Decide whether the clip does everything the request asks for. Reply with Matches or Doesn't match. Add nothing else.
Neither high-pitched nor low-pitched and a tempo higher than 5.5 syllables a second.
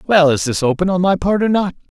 Matches